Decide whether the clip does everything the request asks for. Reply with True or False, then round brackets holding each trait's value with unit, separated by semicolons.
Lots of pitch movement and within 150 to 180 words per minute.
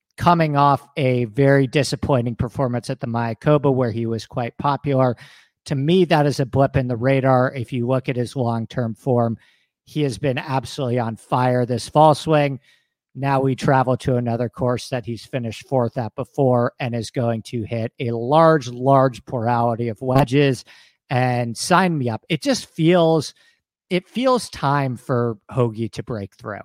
False (2.9 semitones; 175 wpm)